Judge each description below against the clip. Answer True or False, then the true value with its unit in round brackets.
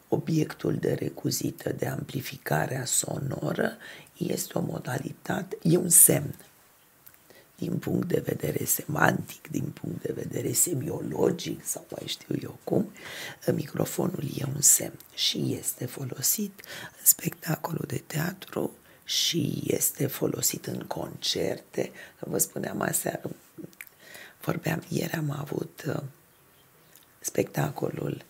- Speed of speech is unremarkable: False (110 wpm)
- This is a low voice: False (160 Hz)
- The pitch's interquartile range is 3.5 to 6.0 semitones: False (2.8 semitones)